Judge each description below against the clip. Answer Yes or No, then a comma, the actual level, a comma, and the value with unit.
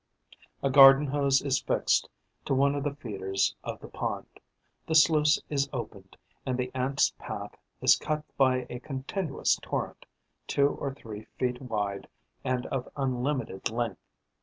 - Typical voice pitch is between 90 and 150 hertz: Yes, low, 135 Hz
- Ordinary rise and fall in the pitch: No, narrow, 2.3 semitones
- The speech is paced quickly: No, average, 150 wpm